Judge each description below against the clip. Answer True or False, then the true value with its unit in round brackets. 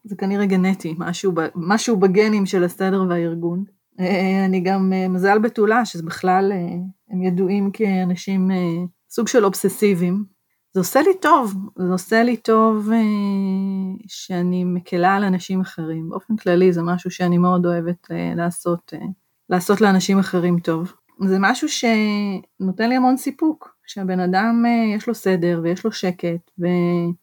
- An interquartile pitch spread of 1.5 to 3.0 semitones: True (2.6 semitones)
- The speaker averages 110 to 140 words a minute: True (135 wpm)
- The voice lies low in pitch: False (190 Hz)